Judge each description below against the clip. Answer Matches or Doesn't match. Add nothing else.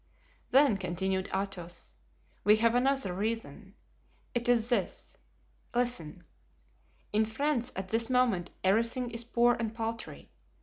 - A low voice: Doesn't match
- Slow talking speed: Matches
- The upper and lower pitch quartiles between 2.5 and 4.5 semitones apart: Matches